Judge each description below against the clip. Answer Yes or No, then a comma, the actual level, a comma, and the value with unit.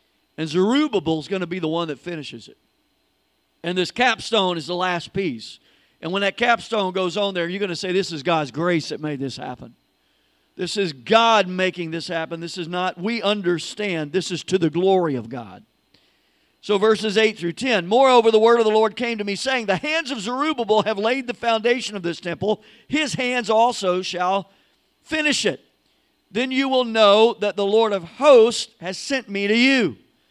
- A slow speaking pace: No, average, 200 wpm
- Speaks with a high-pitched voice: Yes, high, 200 Hz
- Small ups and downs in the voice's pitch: No, average, 4.7 semitones